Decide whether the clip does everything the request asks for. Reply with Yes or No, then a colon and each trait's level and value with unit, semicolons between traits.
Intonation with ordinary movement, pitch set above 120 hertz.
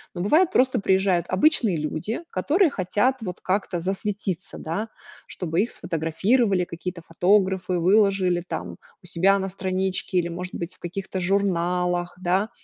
No: narrow, 2.3 semitones; medium, 185 Hz